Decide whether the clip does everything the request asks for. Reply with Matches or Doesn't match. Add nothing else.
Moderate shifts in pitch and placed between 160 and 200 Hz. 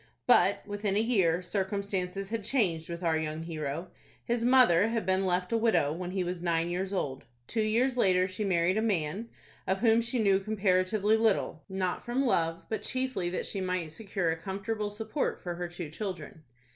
Matches